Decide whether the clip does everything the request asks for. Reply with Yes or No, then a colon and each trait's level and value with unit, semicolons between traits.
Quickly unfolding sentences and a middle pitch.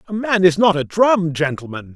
Yes: fast, 215 wpm; medium, 175 Hz